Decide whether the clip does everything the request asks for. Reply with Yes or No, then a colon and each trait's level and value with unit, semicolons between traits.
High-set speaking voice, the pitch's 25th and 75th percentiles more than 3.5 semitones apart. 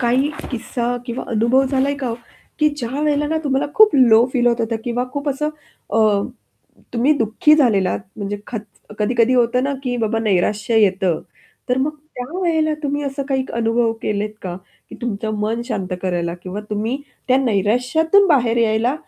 Yes: high, 240 Hz; average, 3.9 semitones